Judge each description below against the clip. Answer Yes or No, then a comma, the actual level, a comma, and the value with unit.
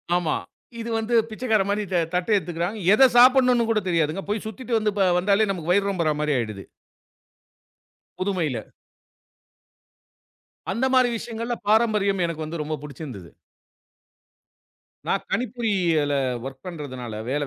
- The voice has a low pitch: No, high, 190 Hz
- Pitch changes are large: Yes, wide, 6.2 semitones